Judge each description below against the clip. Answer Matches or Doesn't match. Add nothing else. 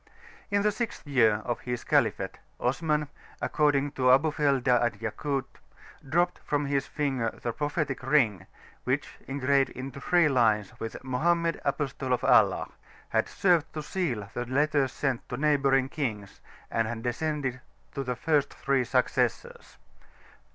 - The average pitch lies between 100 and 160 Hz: Matches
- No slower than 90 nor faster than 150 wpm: Matches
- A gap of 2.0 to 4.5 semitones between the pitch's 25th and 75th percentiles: Matches